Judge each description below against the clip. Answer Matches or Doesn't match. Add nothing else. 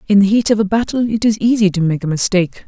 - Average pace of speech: Doesn't match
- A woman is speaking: Matches